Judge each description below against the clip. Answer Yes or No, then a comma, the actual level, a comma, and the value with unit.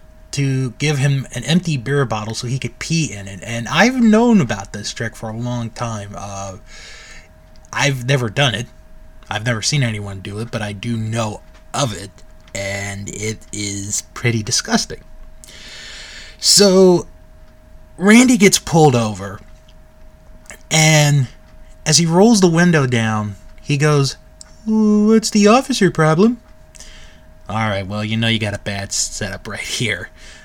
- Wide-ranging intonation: Yes, wide, 6.8 semitones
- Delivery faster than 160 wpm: No, average, 150 wpm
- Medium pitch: No, low, 115 Hz